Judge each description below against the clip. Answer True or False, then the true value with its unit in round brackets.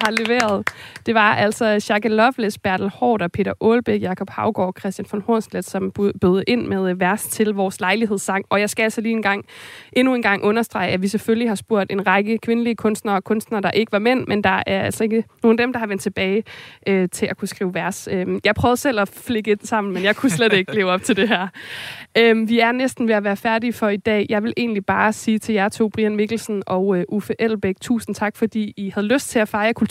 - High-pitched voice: True (210 Hz)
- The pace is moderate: False (240 wpm)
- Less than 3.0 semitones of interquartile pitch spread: True (2.4 semitones)